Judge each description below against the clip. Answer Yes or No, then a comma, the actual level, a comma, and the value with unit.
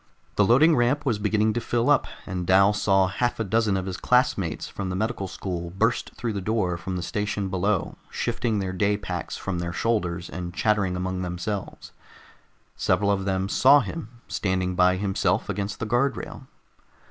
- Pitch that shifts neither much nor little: Yes, average, 3.4 semitones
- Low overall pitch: Yes, low, 100 Hz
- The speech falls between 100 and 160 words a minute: No, average, 180 wpm